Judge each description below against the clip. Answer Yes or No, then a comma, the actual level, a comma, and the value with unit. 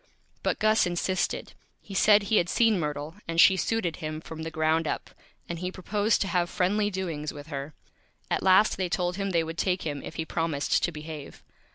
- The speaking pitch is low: No, medium, 175 Hz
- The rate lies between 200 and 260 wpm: Yes, fast, 205 wpm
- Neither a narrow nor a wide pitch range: Yes, average, 3.3 semitones